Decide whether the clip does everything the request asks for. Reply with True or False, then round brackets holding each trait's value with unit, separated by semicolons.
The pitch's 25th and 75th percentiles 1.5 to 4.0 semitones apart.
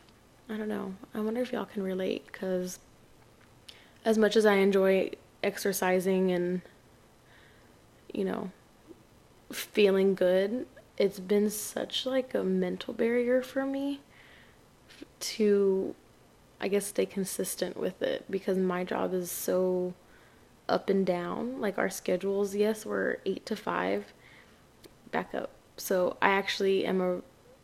True (2.8 semitones)